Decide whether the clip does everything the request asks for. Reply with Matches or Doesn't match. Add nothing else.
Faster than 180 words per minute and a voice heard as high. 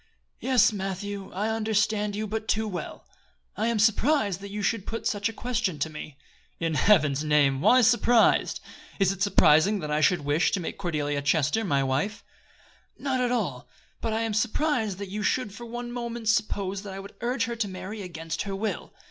Matches